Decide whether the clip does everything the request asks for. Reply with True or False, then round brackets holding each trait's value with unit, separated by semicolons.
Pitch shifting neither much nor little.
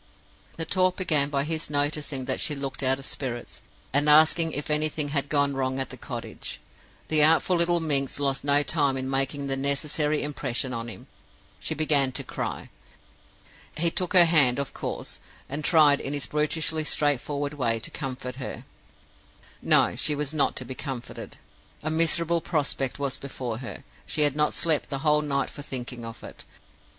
False (2.3 semitones)